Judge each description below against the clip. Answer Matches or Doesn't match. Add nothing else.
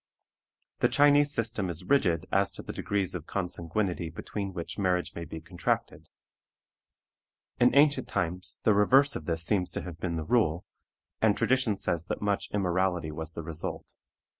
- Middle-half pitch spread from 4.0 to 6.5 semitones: Matches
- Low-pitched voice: Matches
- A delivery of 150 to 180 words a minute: Matches